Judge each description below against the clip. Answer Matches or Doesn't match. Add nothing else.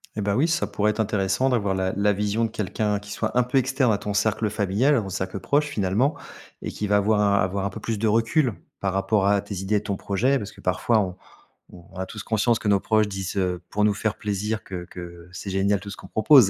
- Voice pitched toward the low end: Matches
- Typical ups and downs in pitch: Doesn't match